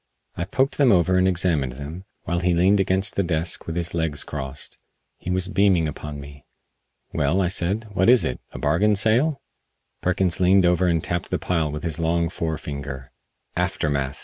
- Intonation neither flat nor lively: Yes, average, 3.8 semitones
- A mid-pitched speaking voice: No, very low, 85 Hz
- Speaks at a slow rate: No, average, 185 wpm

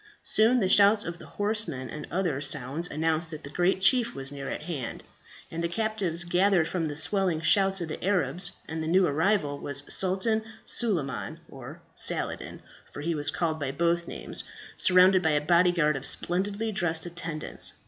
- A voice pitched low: No, medium, 170 Hz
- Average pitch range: Yes, average, 4.0 semitones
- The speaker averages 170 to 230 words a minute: Yes, average, 180 wpm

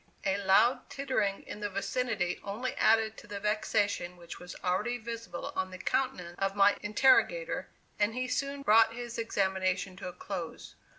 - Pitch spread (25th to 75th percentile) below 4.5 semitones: Yes, average, 3.9 semitones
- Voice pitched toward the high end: Yes, high, 205 Hz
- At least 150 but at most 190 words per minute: Yes, average, 165 wpm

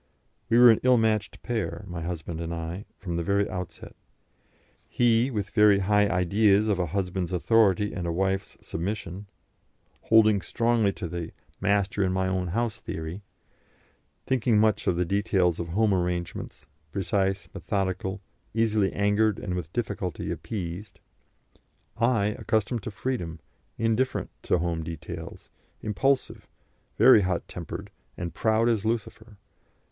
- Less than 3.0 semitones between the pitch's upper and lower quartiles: No, average, 3.6 semitones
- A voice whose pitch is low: Yes, low, 100 Hz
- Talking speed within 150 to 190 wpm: No, average, 140 wpm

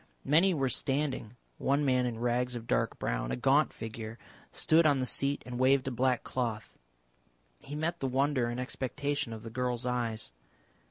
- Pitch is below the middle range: Yes, low, 125 Hz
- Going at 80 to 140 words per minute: No, average, 175 wpm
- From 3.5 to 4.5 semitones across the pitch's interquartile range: No, average, 2.8 semitones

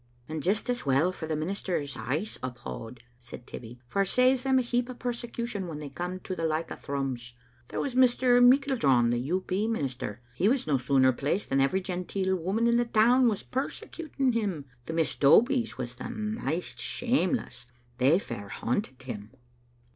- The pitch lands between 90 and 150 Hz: No, medium, 180 Hz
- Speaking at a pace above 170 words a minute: Yes, average, 185 wpm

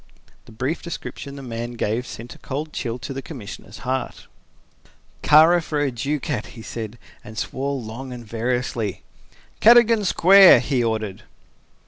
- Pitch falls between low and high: No, low, 130 Hz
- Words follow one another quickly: No, average, 145 wpm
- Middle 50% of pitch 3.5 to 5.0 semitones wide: Yes, average, 4.5 semitones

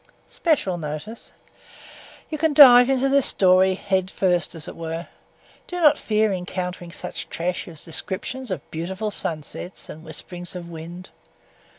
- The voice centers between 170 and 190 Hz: Yes, medium, 185 Hz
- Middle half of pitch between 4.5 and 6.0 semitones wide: Yes, average, 5.1 semitones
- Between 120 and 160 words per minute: Yes, average, 150 wpm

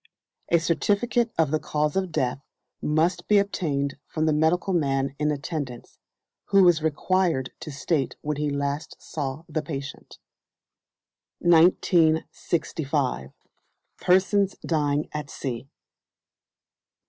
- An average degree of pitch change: Yes, average, 3.6 semitones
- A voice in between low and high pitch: Yes, medium, 155 Hz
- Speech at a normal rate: No, slow, 110 wpm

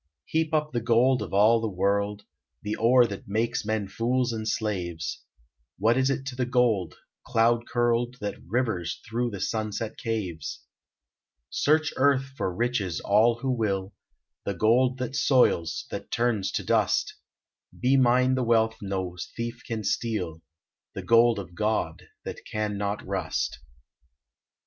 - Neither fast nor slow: Yes, average, 150 wpm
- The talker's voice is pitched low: Yes, low, 115 Hz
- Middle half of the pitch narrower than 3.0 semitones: No, average, 3.4 semitones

